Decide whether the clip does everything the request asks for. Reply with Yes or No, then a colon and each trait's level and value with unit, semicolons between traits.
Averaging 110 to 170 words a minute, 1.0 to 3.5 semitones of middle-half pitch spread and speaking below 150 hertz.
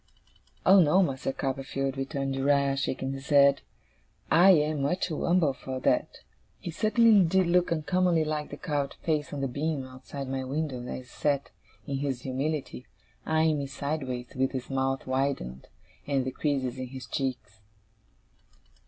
Yes: average, 160 wpm; average, 2.9 semitones; medium, 140 Hz